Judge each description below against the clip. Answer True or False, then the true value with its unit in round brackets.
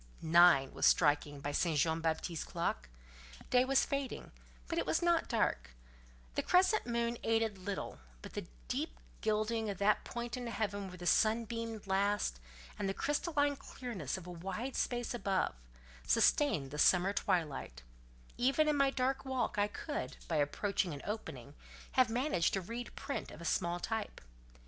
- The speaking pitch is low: False (210 Hz)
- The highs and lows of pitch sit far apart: True (6.2 semitones)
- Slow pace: False (165 wpm)